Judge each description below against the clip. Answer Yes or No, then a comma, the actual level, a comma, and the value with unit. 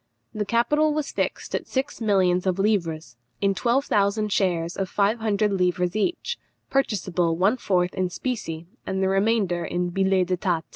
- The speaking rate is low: No, average, 160 wpm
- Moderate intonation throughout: Yes, average, 3.4 semitones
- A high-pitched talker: Yes, high, 195 Hz